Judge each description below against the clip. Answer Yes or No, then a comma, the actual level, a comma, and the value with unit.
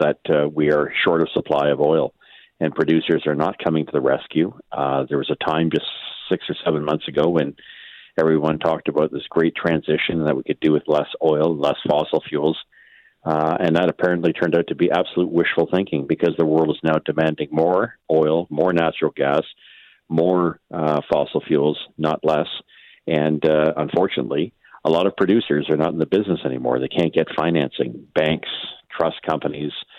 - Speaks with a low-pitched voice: Yes, very low, 80 Hz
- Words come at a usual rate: Yes, average, 185 wpm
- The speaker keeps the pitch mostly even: Yes, narrow, 1.2 semitones